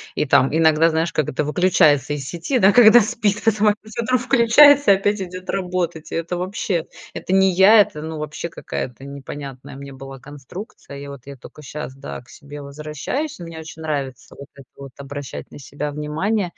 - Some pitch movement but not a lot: No, wide, 5.7 semitones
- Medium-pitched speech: Yes, medium, 160 Hz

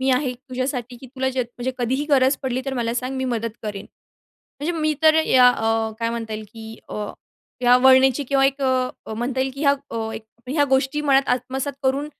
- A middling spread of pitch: No, narrow, 2.2 semitones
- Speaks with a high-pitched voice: Yes, very high, 260 Hz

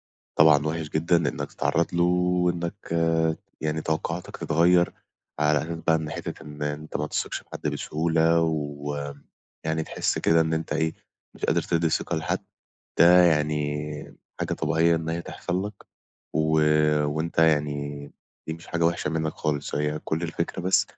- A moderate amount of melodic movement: No, narrow, 1.9 semitones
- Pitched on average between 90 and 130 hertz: No, very low, 80 Hz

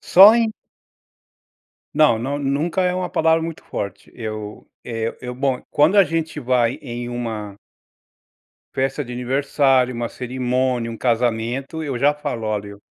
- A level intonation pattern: No, average, 4.1 semitones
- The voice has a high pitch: No, low, 130 Hz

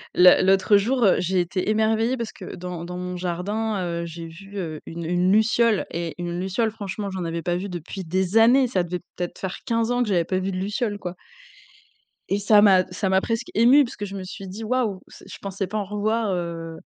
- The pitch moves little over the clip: No, average, 3.4 semitones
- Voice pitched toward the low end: No, high, 190 Hz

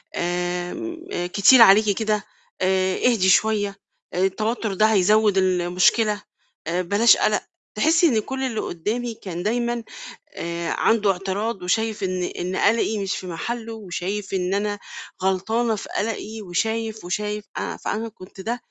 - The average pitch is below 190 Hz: No, high, 205 Hz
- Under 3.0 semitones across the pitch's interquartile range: No, average, 3.3 semitones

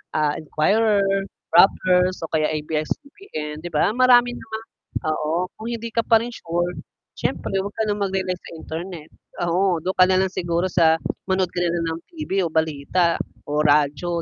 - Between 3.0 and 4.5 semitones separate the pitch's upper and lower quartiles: Yes, average, 3.6 semitones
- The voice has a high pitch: No, medium, 180 Hz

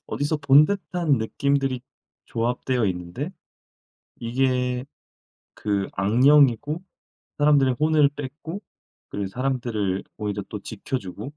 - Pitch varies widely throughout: No, average, 5.0 semitones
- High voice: No, low, 130 Hz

